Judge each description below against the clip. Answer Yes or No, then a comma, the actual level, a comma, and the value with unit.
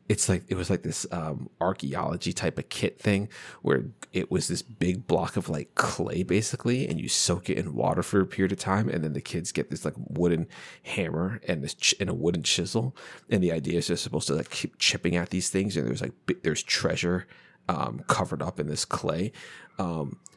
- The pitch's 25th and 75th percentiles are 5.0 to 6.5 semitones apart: No, average, 2.7 semitones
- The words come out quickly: Yes, fast, 220 wpm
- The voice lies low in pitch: Yes, very low, 95 Hz